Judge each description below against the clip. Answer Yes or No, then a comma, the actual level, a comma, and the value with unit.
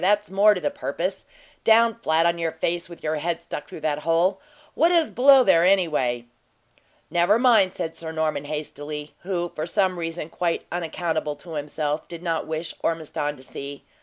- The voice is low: No, medium, 170 Hz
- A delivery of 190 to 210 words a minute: No, average, 180 wpm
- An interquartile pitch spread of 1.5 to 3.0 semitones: No, average, 3.5 semitones